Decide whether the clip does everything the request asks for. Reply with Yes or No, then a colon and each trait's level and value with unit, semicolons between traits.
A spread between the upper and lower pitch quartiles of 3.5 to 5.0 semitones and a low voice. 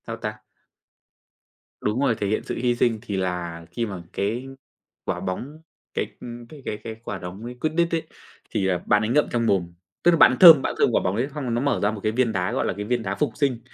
Yes: average, 4.4 semitones; low, 115 Hz